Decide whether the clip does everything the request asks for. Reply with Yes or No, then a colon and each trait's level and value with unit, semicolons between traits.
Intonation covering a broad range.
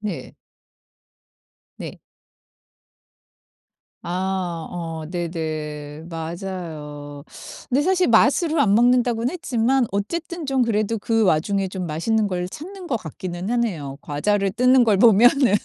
Yes: wide, 6.3 semitones